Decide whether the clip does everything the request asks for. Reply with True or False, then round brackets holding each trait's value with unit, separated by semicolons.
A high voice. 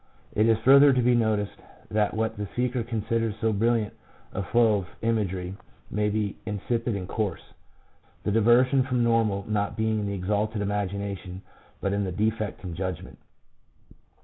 False (105 Hz)